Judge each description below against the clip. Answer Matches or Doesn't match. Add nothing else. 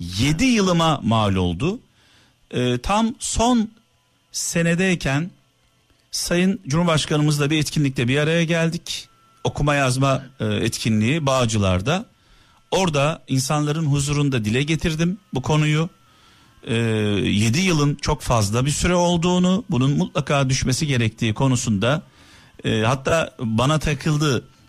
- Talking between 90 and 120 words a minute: Matches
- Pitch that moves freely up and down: Doesn't match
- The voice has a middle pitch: Matches